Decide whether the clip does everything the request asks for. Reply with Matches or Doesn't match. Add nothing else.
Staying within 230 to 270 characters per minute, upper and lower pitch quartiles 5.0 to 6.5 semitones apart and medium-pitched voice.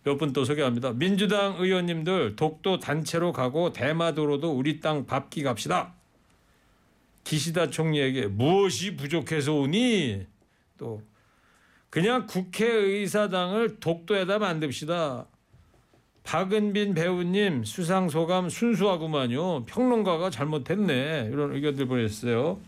Matches